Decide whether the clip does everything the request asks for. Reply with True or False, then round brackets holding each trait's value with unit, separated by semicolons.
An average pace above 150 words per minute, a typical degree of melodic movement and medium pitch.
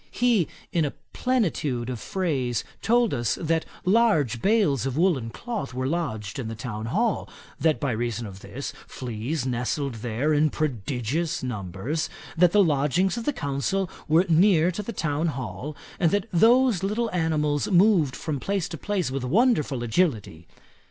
False (160 wpm; 7.0 semitones; 155 Hz)